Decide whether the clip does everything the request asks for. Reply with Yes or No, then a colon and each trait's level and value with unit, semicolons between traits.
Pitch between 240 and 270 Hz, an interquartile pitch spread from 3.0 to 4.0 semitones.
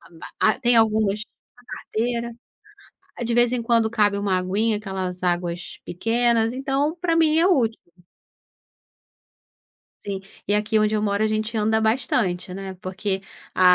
No: high, 215 Hz; average, 3.3 semitones